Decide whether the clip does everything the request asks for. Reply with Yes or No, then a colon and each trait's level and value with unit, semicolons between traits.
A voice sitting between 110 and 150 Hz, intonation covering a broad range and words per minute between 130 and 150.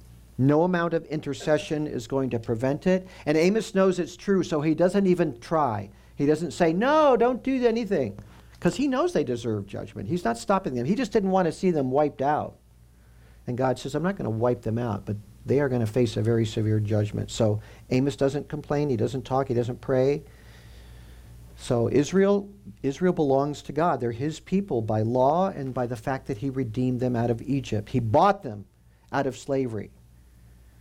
No: low, 135 Hz; wide, 6.6 semitones; average, 200 wpm